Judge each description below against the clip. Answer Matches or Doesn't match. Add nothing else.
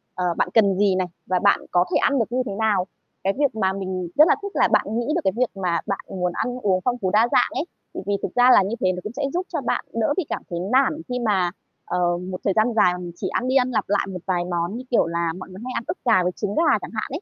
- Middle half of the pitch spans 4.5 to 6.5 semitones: Matches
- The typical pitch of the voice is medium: Doesn't match